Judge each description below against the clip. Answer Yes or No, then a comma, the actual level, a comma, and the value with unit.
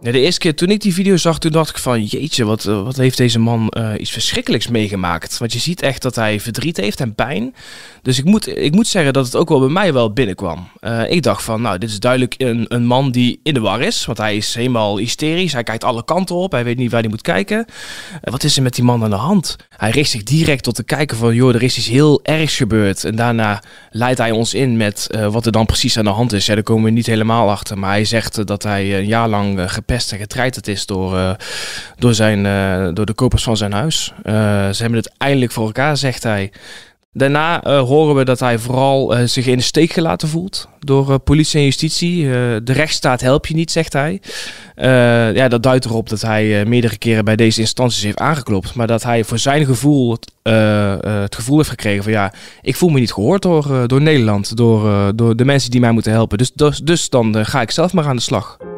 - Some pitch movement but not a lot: Yes, average, 4.1 semitones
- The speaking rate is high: Yes, fast, 250 wpm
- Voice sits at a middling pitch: No, low, 120 Hz